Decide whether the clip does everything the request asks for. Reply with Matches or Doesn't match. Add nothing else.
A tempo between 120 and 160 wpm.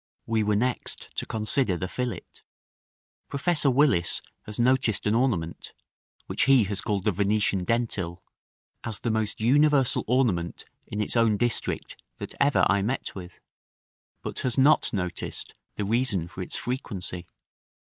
Matches